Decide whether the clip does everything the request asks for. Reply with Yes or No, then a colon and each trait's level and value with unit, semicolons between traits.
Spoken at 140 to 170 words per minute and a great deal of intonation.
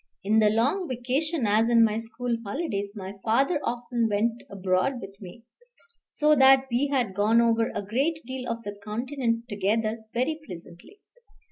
No: average, 160 wpm; average, 3.9 semitones